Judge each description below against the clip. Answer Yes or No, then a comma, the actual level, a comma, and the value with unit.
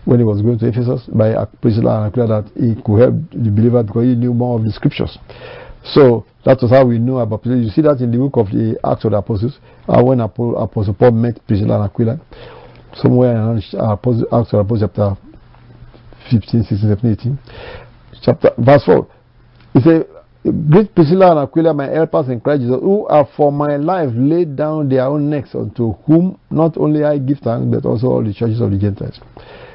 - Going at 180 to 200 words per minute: Yes, average, 195 wpm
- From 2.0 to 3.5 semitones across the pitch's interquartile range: No, average, 4.3 semitones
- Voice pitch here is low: Yes, low, 120 Hz